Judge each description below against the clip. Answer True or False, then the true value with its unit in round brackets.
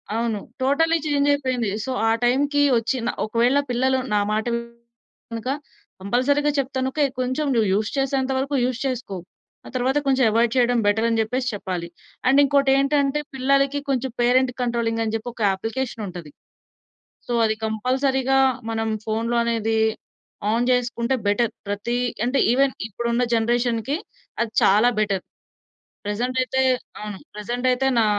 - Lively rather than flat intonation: False (3.0 semitones)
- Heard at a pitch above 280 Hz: False (245 Hz)